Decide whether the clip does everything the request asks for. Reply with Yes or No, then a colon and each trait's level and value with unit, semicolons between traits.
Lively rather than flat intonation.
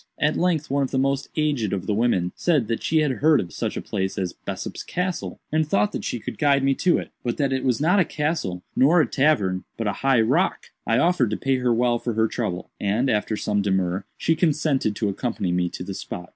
Yes: wide, 6.4 semitones